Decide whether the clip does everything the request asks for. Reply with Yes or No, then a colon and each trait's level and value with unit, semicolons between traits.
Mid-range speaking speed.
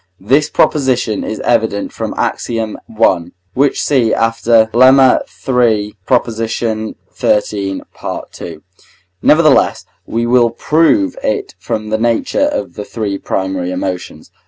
No: slow, 120 wpm